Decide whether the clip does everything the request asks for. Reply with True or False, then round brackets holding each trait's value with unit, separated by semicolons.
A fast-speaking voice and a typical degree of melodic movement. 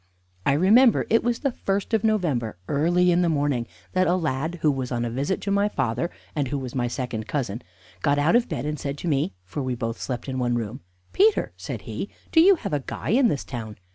False (235 wpm; 7.3 semitones)